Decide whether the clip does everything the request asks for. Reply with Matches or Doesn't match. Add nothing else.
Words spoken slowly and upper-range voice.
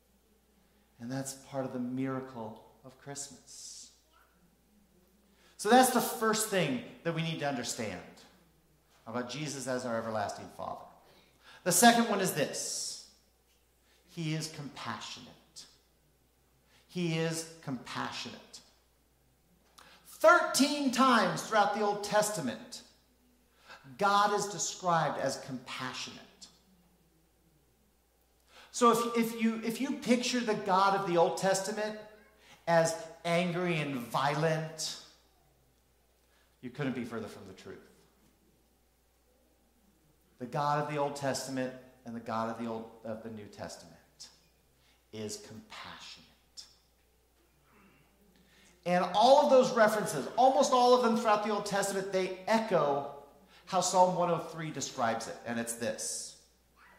Doesn't match